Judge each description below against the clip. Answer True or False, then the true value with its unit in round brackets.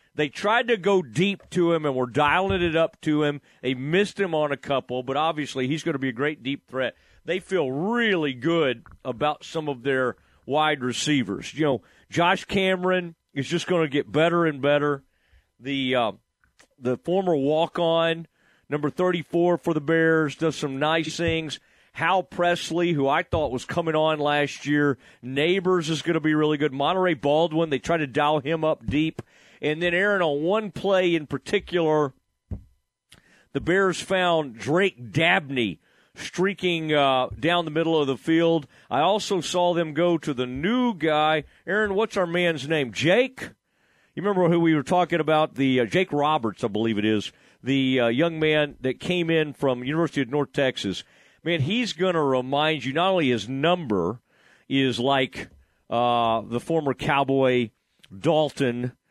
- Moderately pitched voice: True (155 Hz)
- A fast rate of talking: False (175 wpm)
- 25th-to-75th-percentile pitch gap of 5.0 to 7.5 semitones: False (4.3 semitones)